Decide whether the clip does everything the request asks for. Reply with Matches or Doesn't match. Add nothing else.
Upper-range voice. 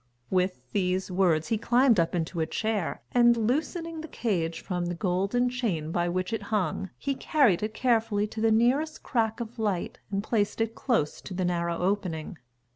Matches